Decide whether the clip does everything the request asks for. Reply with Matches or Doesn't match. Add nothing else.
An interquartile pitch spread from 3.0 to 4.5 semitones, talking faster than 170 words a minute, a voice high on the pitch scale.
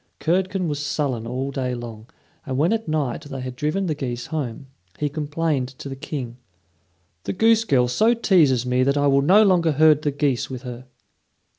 Doesn't match